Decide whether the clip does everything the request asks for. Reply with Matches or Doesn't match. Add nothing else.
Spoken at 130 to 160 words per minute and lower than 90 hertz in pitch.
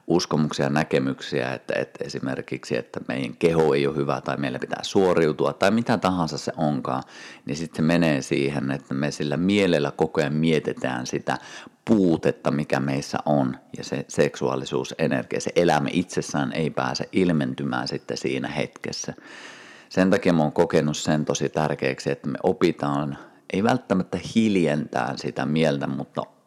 Matches